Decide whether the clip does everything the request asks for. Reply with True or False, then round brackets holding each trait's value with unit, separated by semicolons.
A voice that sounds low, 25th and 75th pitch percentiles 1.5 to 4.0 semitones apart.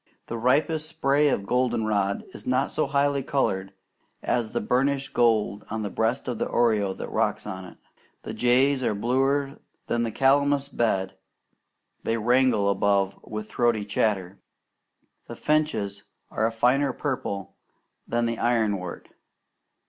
False (120 Hz; 4.8 semitones)